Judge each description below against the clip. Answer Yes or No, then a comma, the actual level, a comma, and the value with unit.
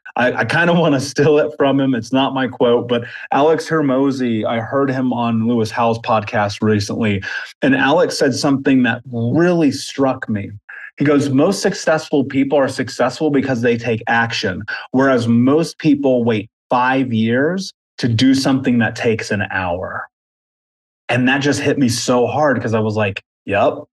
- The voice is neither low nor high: No, low, 130 Hz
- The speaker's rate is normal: Yes, average, 175 wpm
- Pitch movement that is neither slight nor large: Yes, average, 3.2 semitones